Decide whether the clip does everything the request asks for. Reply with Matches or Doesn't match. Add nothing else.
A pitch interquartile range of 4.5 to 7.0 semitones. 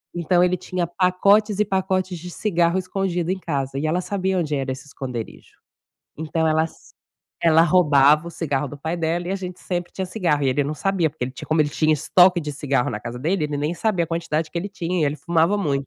Doesn't match